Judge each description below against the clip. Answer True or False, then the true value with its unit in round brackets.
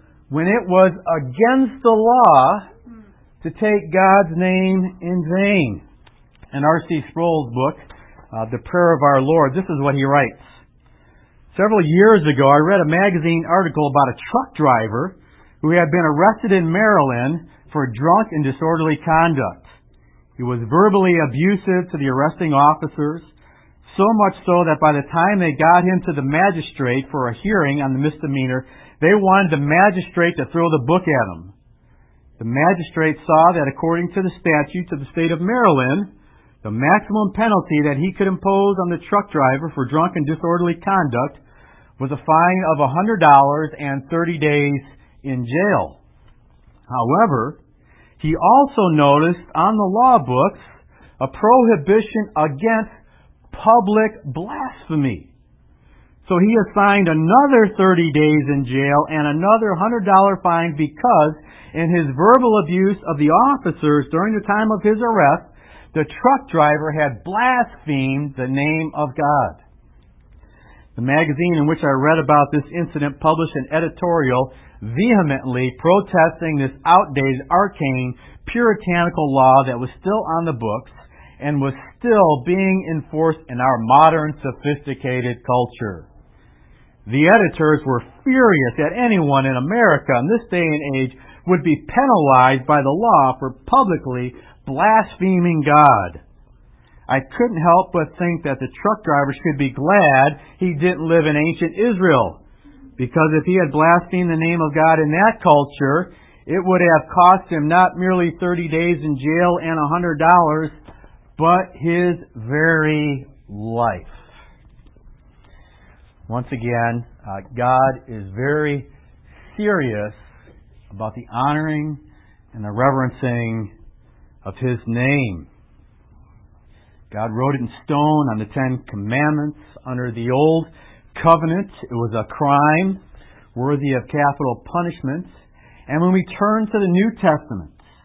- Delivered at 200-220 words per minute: False (140 wpm)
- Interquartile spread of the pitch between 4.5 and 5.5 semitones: True (5.2 semitones)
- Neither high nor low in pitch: True (155 Hz)